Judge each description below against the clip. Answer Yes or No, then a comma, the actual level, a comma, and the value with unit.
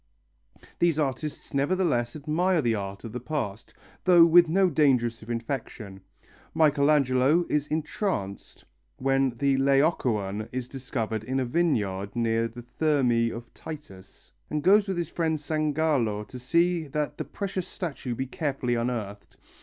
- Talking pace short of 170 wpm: Yes, average, 140 wpm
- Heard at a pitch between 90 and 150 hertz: Yes, low, 135 Hz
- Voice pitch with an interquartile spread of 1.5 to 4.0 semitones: No, average, 5.2 semitones